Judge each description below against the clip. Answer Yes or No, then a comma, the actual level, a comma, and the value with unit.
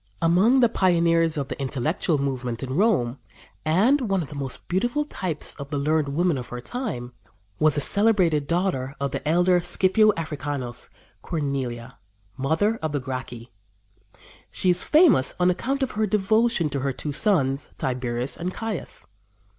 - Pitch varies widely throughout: Yes, wide, 6.0 semitones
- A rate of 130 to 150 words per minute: No, average, 160 wpm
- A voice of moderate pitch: Yes, medium, 160 Hz